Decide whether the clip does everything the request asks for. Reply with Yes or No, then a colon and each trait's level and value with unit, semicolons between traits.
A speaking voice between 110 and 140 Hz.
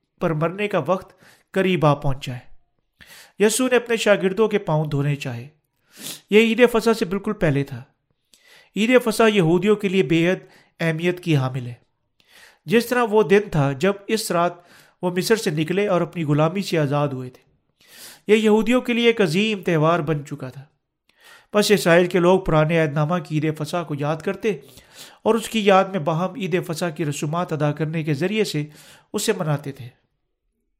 No: medium, 175 Hz